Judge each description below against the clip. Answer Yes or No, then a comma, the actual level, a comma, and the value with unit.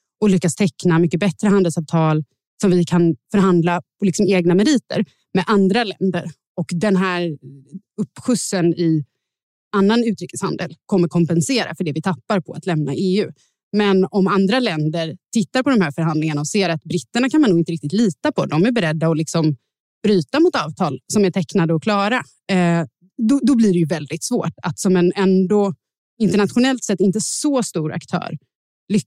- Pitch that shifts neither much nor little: Yes, average, 3.7 semitones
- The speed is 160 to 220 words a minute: Yes, average, 175 wpm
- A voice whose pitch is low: No, medium, 185 Hz